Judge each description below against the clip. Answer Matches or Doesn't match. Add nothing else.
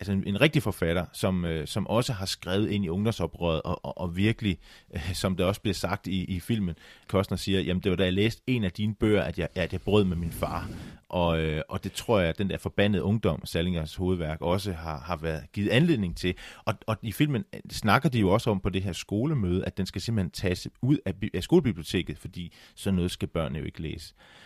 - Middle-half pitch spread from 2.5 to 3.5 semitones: Matches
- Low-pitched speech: Matches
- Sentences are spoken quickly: Matches